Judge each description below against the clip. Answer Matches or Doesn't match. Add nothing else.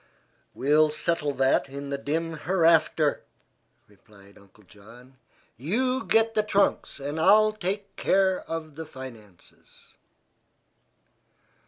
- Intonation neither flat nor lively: Doesn't match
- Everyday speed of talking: Doesn't match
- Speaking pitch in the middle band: Matches